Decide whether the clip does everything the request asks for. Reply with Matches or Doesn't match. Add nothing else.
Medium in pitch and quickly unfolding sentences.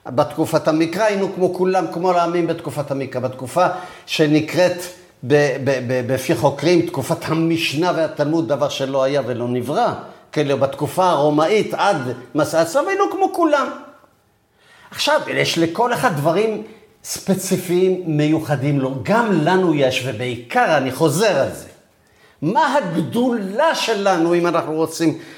Doesn't match